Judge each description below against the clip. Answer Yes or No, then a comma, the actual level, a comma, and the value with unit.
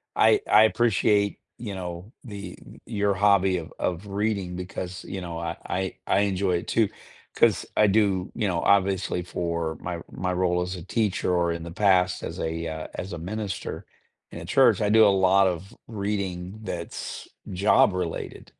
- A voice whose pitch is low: Yes, very low, 95 Hz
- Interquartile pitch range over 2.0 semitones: Yes, narrow, 2.4 semitones